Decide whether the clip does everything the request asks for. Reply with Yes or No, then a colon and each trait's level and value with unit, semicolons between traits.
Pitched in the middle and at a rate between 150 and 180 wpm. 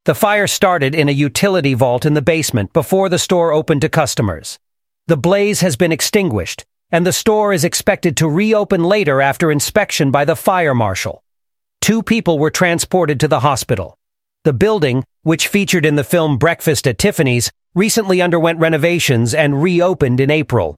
Yes: medium, 165 Hz; average, 170 wpm